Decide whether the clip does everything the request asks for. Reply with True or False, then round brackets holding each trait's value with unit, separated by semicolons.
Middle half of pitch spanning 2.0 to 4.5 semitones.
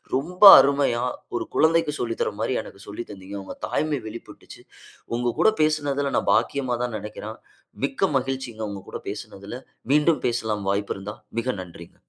False (5.2 semitones)